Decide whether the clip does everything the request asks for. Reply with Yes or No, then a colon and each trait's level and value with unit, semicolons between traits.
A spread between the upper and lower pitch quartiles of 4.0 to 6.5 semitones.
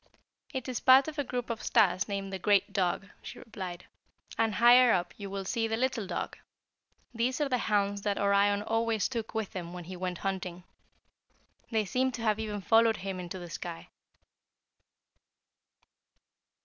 No: average, 3.5 semitones